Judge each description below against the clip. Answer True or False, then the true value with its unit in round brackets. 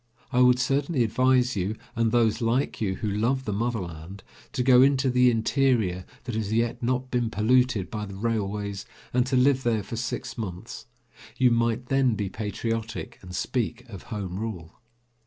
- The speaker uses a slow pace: False (175 wpm)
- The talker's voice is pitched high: False (115 Hz)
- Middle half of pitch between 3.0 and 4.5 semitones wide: True (3.3 semitones)